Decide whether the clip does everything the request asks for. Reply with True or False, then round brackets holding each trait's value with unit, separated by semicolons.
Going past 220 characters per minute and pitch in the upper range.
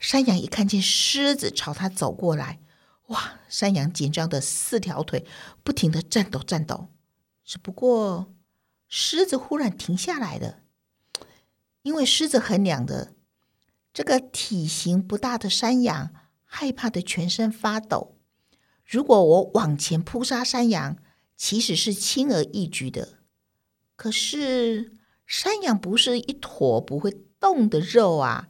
False (195 characters per minute; 205 Hz)